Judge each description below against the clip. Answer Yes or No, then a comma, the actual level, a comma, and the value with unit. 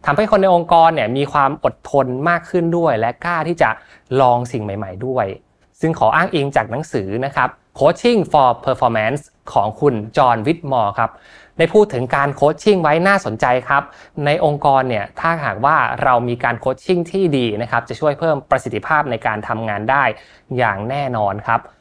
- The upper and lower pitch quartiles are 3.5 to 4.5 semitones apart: No, average, 5.2 semitones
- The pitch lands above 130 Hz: Yes, medium, 140 Hz